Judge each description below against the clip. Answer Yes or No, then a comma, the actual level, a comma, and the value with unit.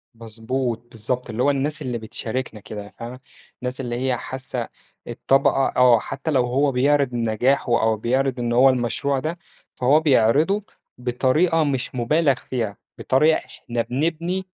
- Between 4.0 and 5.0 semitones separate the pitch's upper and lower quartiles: No, average, 2.9 semitones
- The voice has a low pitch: Yes, low, 130 Hz